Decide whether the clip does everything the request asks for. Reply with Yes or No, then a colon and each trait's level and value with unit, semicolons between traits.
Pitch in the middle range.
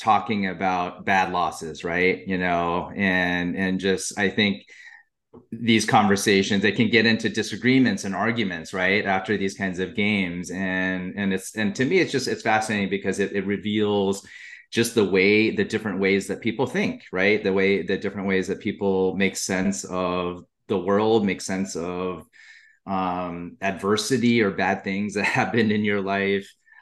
No: low, 100 Hz